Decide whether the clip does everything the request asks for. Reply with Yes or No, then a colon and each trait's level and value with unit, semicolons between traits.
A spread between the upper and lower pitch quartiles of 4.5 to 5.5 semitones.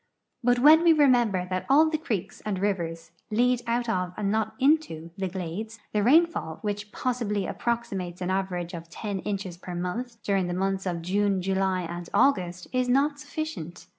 Yes: average, 5.2 semitones